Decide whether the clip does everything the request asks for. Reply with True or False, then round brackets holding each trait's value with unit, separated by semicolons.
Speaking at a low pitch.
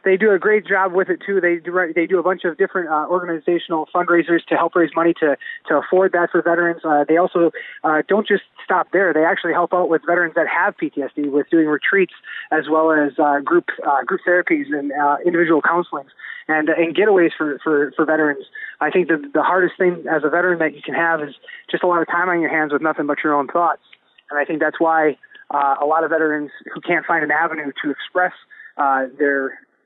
False (165 Hz)